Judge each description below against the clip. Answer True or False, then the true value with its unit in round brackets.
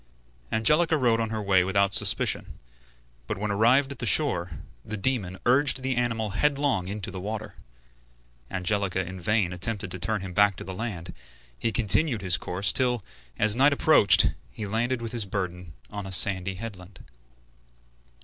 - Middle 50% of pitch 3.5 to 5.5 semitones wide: True (4.2 semitones)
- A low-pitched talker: True (105 Hz)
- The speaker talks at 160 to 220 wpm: True (165 wpm)